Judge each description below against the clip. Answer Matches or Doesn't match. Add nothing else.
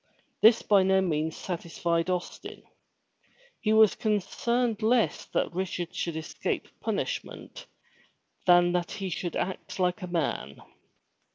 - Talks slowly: Matches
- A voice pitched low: Doesn't match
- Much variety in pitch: Doesn't match